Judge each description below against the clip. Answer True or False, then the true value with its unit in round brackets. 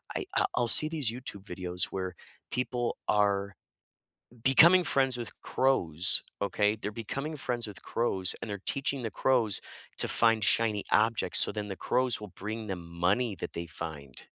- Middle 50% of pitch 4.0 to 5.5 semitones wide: True (4.5 semitones)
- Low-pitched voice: True (110 Hz)